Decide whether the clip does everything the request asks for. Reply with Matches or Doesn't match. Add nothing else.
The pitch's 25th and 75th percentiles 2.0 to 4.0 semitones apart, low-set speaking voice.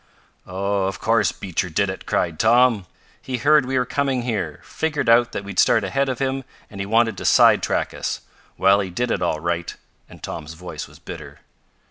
Doesn't match